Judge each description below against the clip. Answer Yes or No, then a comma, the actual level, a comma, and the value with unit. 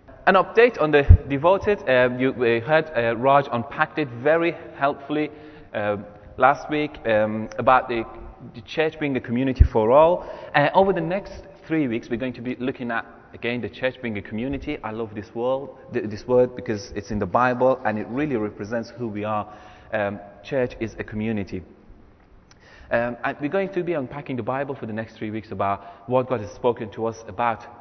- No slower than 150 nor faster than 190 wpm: No, average, 200 wpm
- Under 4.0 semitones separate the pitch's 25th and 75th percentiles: No, average, 4.6 semitones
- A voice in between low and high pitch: No, low, 125 Hz